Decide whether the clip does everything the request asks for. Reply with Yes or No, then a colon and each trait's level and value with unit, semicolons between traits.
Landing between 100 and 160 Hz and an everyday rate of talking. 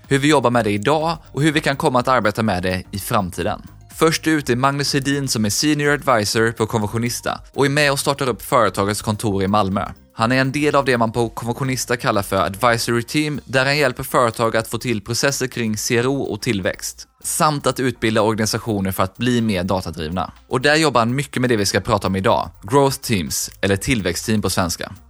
No: low, 120 Hz; fast, 215 wpm